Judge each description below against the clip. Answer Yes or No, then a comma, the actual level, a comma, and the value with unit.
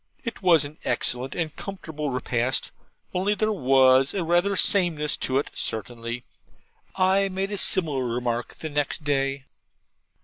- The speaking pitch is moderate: Yes, medium, 150 Hz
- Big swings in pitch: Yes, wide, 6.2 semitones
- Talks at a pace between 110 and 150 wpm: Yes, average, 140 wpm